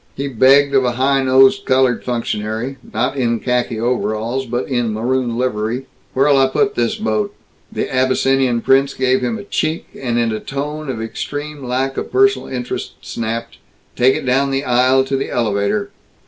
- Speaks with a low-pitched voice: Yes, low, 130 Hz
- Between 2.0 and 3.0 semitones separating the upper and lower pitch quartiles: Yes, narrow, 2.4 semitones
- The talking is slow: No, average, 175 wpm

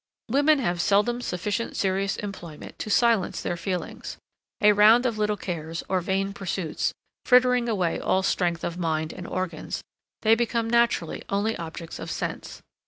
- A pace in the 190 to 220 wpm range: No, average, 155 wpm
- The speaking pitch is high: Yes, high, 195 Hz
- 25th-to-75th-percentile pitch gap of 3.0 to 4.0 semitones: No, average, 4.6 semitones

